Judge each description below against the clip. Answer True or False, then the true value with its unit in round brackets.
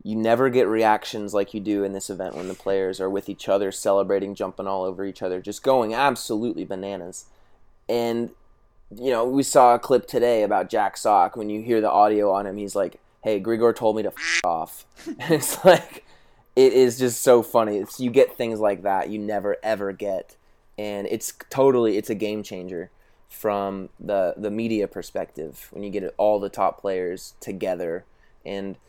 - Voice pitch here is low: True (105 Hz)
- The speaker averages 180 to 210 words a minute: True (195 wpm)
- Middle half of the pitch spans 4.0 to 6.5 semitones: False (2.7 semitones)